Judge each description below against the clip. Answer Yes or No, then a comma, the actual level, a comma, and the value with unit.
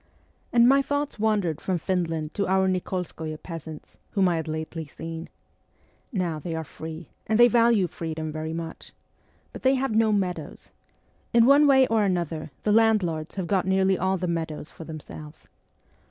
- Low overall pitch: No, medium, 180 Hz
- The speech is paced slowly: No, average, 170 wpm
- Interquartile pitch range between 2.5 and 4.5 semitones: No, average, 5.0 semitones